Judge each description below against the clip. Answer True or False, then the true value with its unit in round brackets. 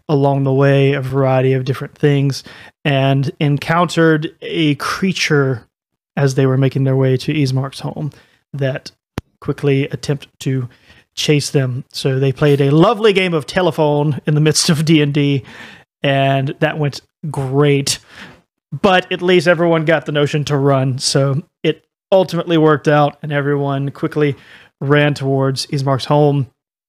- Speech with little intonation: True (2.2 semitones)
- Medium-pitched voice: True (145 Hz)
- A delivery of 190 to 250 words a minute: False (145 wpm)